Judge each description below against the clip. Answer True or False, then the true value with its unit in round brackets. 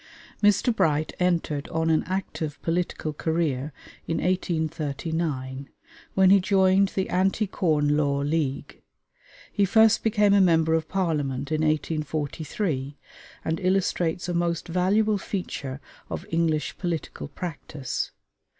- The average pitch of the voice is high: False (165 Hz)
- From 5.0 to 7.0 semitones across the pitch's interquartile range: False (3.8 semitones)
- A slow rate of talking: True (120 wpm)